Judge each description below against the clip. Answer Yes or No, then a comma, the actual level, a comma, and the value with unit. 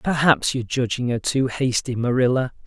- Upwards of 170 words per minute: No, average, 155 wpm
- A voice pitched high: No, low, 125 Hz